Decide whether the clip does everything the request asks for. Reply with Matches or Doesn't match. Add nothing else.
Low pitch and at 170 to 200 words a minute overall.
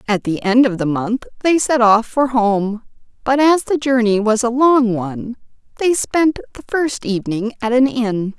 Doesn't match